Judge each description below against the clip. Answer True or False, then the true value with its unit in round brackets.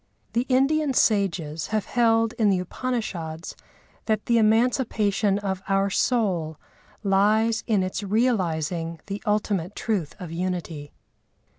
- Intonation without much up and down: False (3.9 semitones)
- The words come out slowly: True (120 wpm)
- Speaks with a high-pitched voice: True (205 Hz)